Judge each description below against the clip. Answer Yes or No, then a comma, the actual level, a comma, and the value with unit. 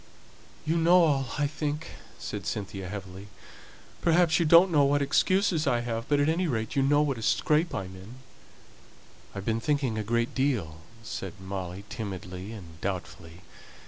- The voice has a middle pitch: No, low, 120 Hz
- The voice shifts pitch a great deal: Yes, wide, 7.5 semitones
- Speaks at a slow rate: No, average, 170 wpm